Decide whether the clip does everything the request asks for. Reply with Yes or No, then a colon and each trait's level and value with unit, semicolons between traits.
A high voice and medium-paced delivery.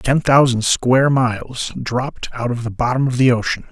No: low, 125 Hz; average, 195 wpm